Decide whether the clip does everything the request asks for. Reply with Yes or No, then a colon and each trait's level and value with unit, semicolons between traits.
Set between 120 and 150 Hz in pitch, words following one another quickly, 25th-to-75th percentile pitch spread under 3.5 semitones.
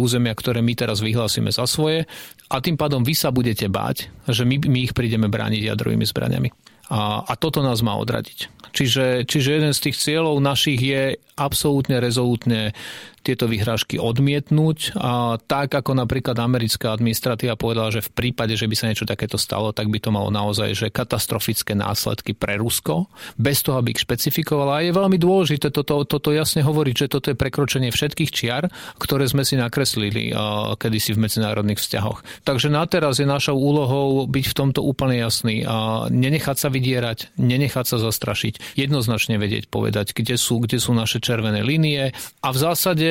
No: low, 125 Hz; fast, 175 wpm; average, 4.1 semitones